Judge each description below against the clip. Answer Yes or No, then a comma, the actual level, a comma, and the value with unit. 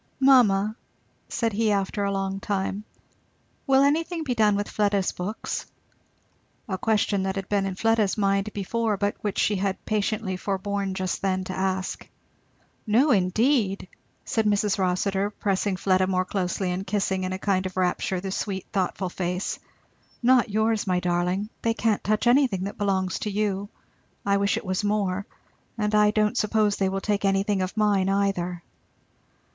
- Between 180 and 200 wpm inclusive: No, average, 165 wpm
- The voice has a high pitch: Yes, high, 200 Hz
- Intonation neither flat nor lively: No, narrow, 2.0 semitones